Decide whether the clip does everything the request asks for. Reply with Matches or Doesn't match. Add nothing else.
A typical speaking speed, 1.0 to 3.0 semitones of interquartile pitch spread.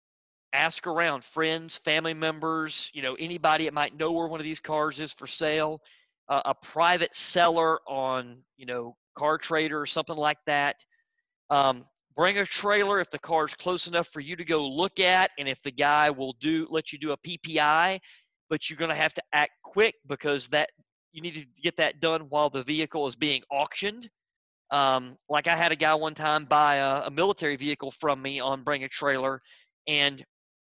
Matches